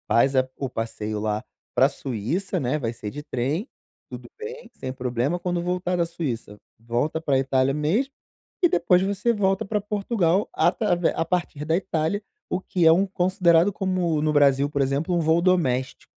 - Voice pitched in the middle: Yes, medium, 165 Hz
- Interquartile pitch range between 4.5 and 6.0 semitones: Yes, wide, 5.6 semitones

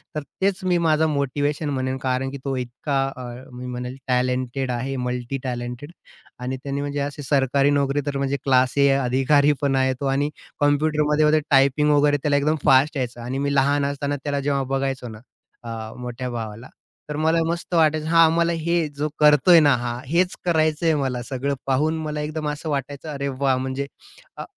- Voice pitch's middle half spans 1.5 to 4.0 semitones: Yes, narrow, 2.5 semitones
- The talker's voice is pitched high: No, medium, 140 Hz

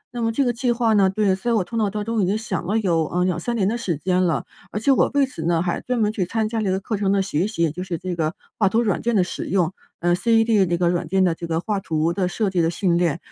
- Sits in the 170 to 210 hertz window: Yes, high, 190 Hz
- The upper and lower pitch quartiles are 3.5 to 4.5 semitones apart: Yes, average, 4.1 semitones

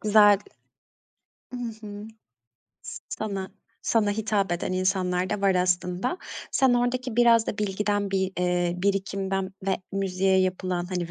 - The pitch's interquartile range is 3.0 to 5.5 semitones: No, narrow, 2.4 semitones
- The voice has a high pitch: Yes, high, 195 Hz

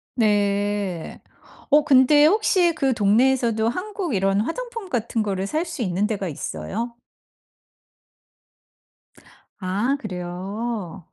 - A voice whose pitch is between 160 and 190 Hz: No, high, 225 Hz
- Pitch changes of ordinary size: No, wide, 6.4 semitones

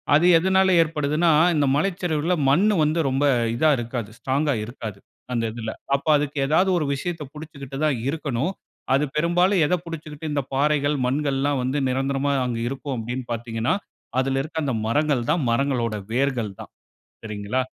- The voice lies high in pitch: No, medium, 140 Hz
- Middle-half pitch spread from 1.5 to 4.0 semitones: Yes, average, 3.6 semitones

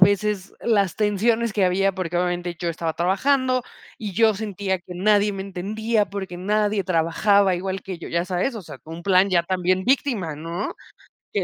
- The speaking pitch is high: Yes, high, 195 Hz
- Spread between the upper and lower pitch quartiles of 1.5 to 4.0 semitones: Yes, average, 2.9 semitones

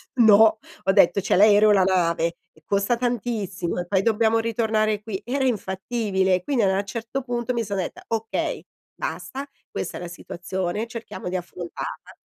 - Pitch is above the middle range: Yes, high, 210 Hz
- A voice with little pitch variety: No, average, 3.4 semitones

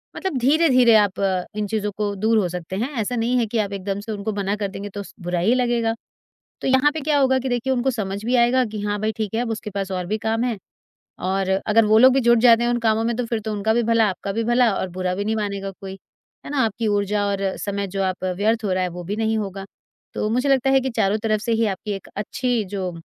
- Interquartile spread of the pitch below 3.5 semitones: Yes, average, 3.1 semitones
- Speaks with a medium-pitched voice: No, high, 220 Hz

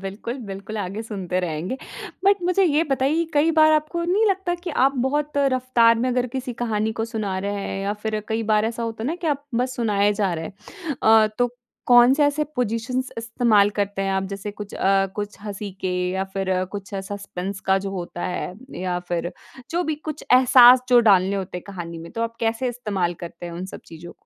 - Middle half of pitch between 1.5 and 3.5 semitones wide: No, average, 5.0 semitones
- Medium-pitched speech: No, high, 220 Hz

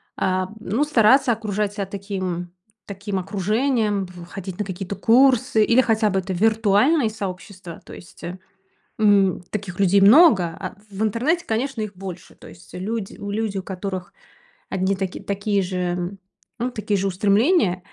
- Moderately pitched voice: No, high, 200 Hz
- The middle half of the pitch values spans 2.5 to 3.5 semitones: Yes, average, 2.9 semitones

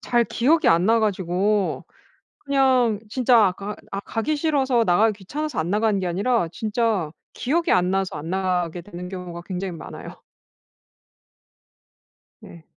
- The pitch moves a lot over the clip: No, average, 4.9 semitones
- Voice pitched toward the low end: No, high, 205 Hz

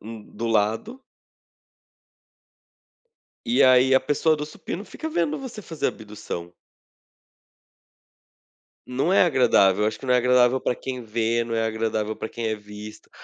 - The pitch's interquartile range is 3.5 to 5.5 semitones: Yes, average, 3.9 semitones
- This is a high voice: No, low, 120 Hz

